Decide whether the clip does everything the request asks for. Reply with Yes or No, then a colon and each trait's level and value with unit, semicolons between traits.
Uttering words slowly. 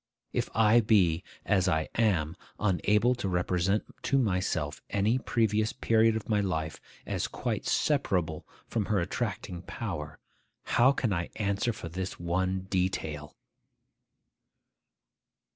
Yes: slow, 125 wpm